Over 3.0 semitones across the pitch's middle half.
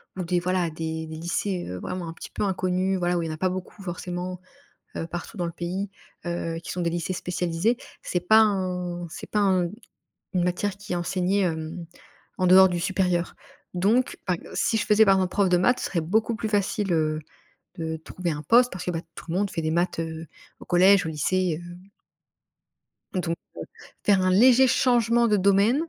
No: narrow, 2.5 semitones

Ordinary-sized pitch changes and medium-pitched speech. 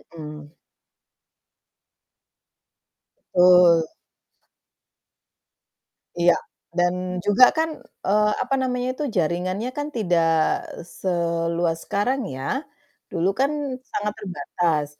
No: wide, 6.4 semitones; medium, 180 Hz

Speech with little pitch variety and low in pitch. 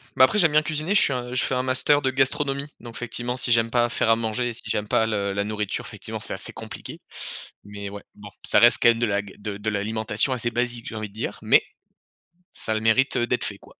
No: average, 3.1 semitones; low, 115 Hz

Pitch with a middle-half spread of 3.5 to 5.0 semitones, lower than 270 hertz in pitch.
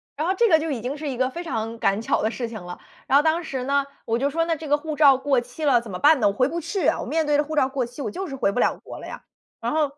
No: average, 4.4 semitones; very high, 280 Hz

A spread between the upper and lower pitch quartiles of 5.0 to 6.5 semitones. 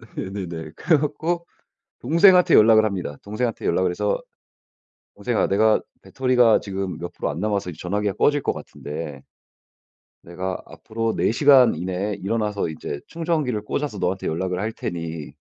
Yes: wide, 5.6 semitones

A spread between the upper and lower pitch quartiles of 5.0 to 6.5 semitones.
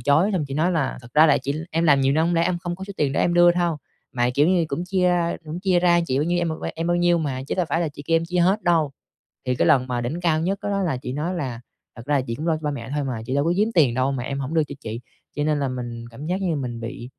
No: average, 4.4 semitones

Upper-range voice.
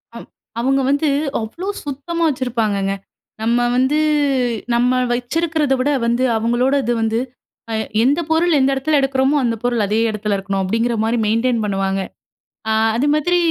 Yes: high, 245 Hz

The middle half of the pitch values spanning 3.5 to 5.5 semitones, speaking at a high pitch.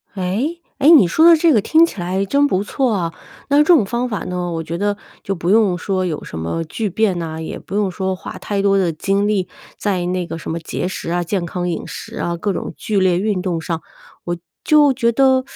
Yes: average, 4.2 semitones; high, 195 Hz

